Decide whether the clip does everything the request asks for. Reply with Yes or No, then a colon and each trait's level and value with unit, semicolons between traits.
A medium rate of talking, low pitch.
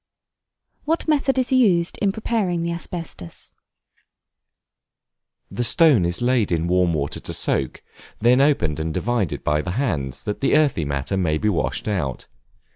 Yes: average, 150 wpm; low, 110 Hz